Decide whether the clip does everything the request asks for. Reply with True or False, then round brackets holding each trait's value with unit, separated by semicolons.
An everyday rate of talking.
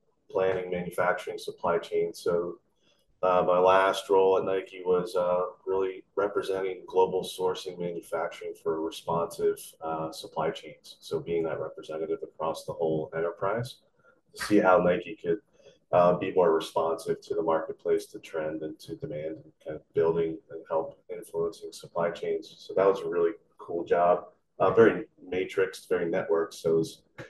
True (160 wpm)